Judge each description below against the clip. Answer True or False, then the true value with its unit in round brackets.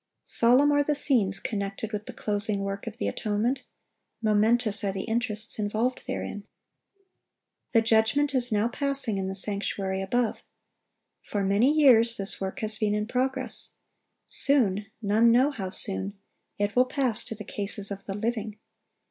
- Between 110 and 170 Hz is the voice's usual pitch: False (215 Hz)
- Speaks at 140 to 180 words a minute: True (150 wpm)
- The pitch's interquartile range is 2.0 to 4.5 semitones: True (3.4 semitones)